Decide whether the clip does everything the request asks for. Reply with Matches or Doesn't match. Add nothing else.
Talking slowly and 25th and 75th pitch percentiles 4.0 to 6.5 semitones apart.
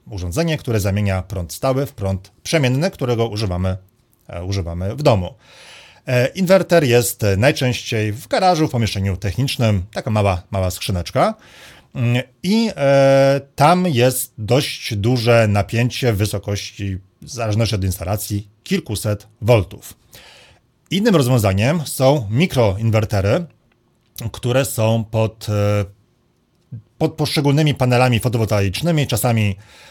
Matches